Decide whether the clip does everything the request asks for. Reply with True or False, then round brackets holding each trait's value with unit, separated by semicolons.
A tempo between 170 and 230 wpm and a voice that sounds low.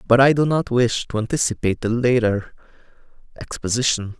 False (145 wpm; 120 Hz)